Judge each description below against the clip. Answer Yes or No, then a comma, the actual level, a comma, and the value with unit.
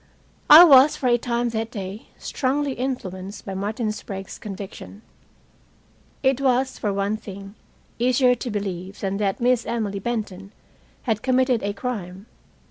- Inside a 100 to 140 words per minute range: Yes, slow, 135 wpm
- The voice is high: Yes, high, 215 Hz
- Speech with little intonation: No, average, 4.2 semitones